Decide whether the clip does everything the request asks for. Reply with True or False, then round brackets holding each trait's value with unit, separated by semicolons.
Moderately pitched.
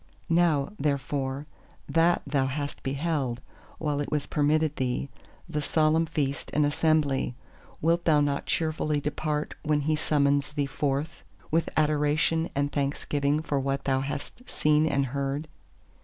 True (145 Hz)